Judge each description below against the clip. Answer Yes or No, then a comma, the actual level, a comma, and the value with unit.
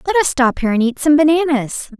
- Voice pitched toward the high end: Yes, very high, 280 Hz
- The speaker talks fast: Yes, fast, 240 wpm